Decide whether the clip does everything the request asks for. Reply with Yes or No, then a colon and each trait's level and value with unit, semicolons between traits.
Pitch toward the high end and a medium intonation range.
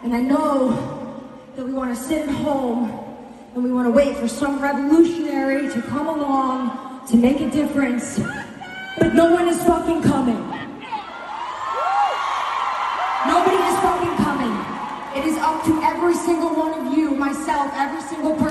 Yes: very high, 280 Hz; average, 3.1 semitones